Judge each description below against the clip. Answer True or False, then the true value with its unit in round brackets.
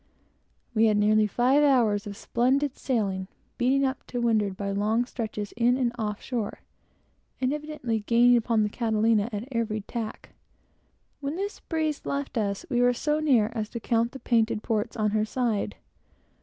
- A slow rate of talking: False (170 wpm)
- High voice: True (230 Hz)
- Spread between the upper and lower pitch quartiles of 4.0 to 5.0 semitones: False (3.1 semitones)